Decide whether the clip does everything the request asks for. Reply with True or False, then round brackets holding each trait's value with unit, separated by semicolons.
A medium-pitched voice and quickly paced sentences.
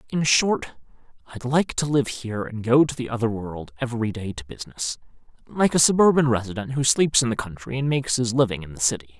False (120 Hz; 215 wpm)